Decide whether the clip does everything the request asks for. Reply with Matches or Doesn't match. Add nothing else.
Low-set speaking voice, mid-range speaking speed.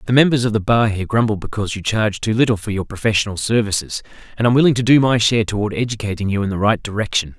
Doesn't match